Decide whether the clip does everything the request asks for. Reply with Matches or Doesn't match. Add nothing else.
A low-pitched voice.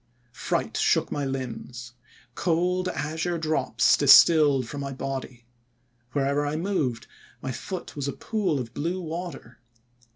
Doesn't match